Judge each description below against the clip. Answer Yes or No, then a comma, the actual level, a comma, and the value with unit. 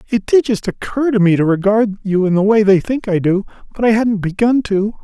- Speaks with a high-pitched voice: Yes, high, 210 Hz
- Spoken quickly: Yes, fast, 250 wpm